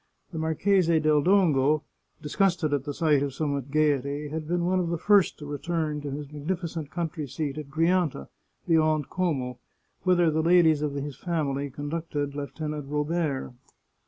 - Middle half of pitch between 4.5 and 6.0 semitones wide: No, average, 2.8 semitones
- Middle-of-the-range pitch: Yes, medium, 155 Hz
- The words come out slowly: No, average, 160 wpm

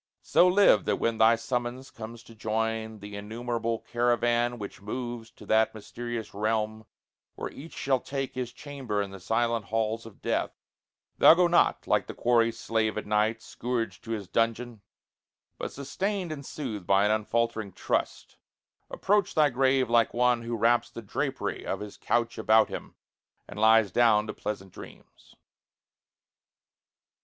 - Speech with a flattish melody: Yes, narrow, 2.1 semitones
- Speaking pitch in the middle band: No, low, 115 Hz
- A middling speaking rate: Yes, average, 155 wpm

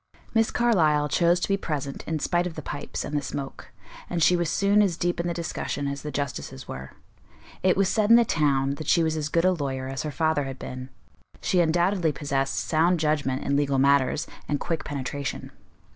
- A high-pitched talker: No, medium, 155 Hz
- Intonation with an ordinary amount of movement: Yes, average, 3.7 semitones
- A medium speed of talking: No, fast, 210 wpm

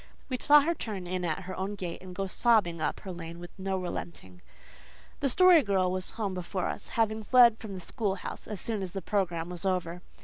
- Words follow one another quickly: Yes, fast, 215 wpm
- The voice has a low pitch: No, high, 190 Hz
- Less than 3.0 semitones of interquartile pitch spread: No, average, 3.4 semitones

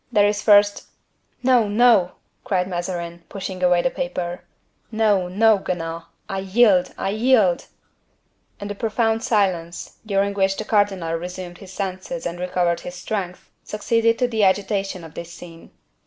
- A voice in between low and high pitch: No, high, 195 Hz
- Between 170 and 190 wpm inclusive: No, average, 150 wpm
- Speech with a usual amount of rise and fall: Yes, average, 3.2 semitones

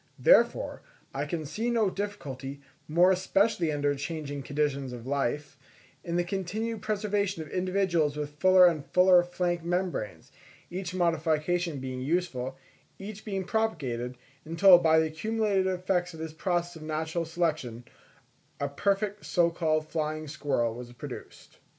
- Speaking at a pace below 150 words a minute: Yes, average, 140 wpm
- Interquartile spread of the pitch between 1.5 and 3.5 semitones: No, average, 4.2 semitones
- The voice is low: No, medium, 170 Hz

